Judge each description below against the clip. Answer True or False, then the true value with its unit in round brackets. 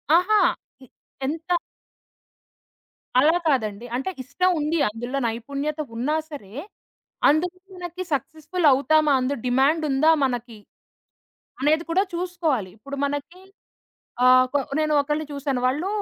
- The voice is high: True (290 Hz)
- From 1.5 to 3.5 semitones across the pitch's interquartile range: False (3.9 semitones)